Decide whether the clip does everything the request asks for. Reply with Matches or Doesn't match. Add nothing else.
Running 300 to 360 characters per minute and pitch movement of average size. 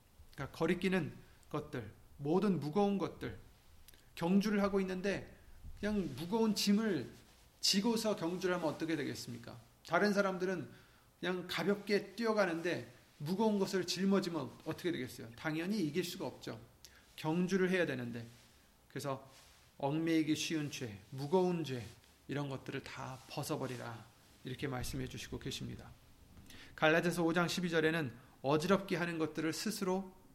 Doesn't match